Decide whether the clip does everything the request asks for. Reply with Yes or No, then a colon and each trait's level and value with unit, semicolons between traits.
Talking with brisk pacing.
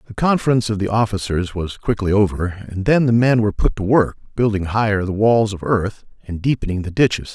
Yes: fast, 210 wpm